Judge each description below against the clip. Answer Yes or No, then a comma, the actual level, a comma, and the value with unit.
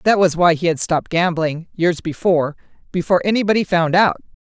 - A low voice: No, medium, 175 Hz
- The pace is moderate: Yes, average, 175 wpm